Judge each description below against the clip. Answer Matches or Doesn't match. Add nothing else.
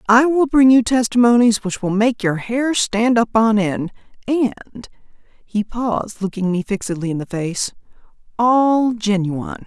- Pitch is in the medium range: Doesn't match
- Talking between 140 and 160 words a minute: Matches